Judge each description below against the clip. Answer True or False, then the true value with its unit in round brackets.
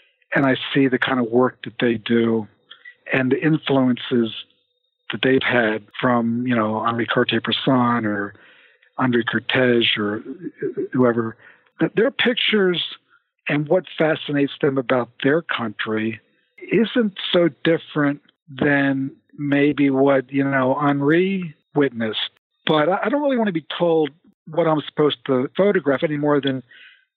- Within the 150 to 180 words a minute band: False (135 wpm)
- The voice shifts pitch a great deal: True (5.9 semitones)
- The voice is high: False (140 Hz)